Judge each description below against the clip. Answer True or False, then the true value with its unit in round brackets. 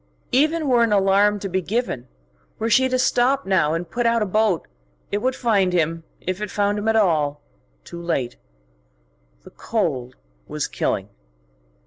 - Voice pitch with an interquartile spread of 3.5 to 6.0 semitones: True (5.3 semitones)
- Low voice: False (205 Hz)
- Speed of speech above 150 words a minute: True (165 wpm)